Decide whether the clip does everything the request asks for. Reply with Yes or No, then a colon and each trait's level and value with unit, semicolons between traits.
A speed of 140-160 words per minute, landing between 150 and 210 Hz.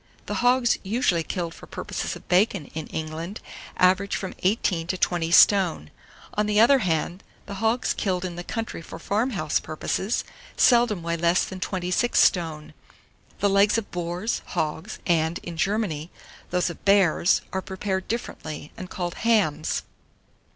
Yes: average, 155 wpm; medium, 185 Hz